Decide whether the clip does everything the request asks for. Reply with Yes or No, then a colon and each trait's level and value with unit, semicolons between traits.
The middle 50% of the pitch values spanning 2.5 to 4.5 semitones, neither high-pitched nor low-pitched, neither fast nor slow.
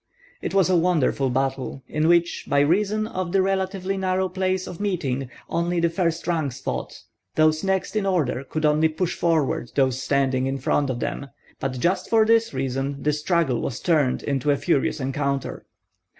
No: average, 5.3 semitones; medium, 160 Hz; average, 180 wpm